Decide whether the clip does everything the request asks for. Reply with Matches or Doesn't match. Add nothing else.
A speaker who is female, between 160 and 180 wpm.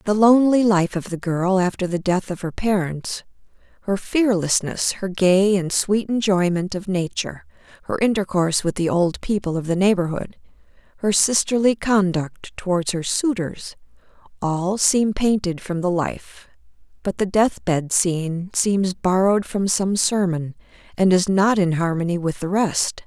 Doesn't match